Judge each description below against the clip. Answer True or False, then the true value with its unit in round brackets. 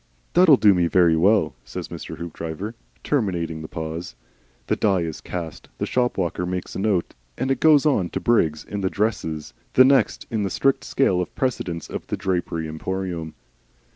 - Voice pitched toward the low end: True (90 Hz)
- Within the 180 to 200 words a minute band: True (185 wpm)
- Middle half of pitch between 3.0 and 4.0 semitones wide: False (5.2 semitones)